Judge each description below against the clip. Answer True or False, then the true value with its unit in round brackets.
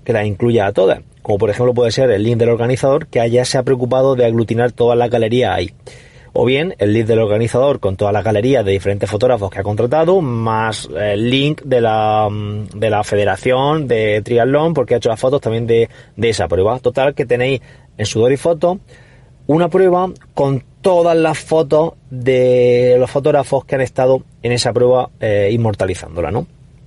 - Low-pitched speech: True (125 Hz)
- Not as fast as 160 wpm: False (190 wpm)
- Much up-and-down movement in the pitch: False (3.4 semitones)